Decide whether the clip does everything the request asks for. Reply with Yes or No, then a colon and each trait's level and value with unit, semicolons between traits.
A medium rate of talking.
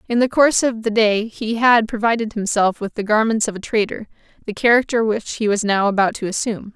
No: fast, 220 wpm